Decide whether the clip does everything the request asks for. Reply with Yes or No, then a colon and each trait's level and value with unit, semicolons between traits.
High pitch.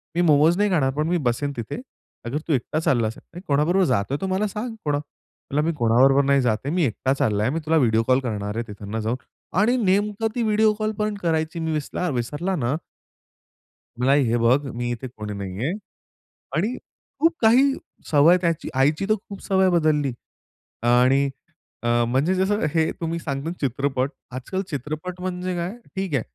No: medium, 150 Hz